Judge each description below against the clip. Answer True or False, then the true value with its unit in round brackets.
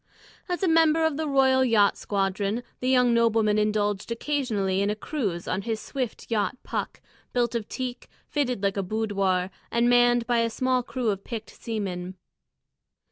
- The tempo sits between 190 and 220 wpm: False (170 wpm)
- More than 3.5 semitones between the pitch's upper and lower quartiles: True (3.9 semitones)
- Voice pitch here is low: False (230 Hz)